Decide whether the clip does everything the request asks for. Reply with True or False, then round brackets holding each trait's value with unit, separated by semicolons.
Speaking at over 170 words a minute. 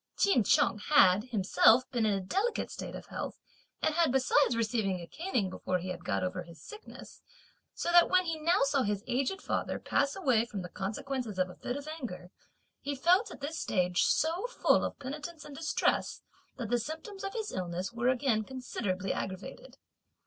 True (190 wpm)